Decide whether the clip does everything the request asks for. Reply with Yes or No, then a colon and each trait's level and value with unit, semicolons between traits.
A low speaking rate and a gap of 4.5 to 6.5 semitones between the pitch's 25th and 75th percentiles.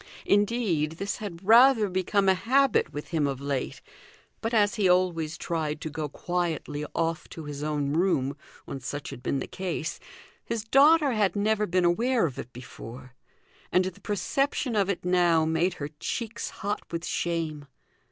No: average, 170 wpm; wide, 5.4 semitones